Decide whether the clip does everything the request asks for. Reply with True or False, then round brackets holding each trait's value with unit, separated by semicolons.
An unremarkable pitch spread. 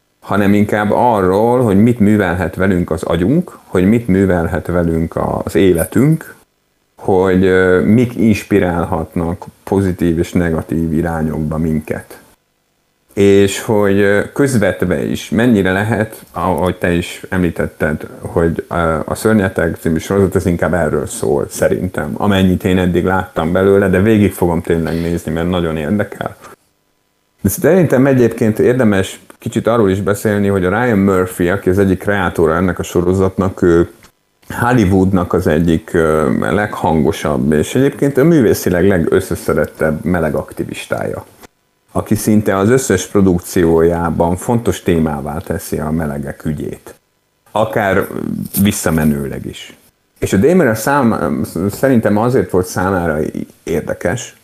True (3.2 semitones)